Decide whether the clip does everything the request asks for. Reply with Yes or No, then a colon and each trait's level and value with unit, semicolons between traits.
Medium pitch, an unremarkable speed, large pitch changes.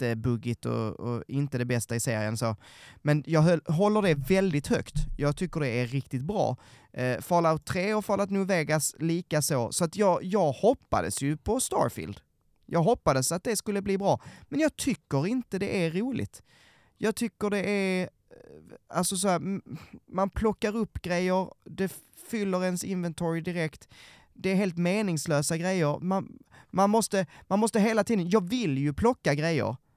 Yes: medium, 175 Hz; average, 170 wpm; wide, 6.3 semitones